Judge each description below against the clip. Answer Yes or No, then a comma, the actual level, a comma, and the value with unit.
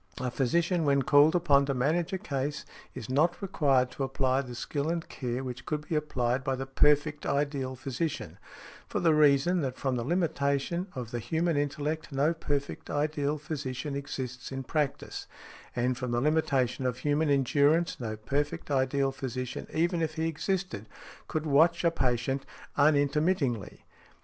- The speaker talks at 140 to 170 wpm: Yes, average, 160 wpm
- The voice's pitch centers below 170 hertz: Yes, medium, 140 Hz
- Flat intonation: No, average, 3.1 semitones